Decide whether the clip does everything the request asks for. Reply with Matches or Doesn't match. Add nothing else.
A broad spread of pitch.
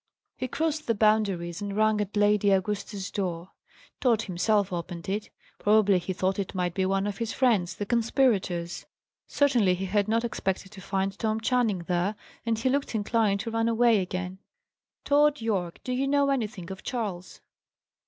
Doesn't match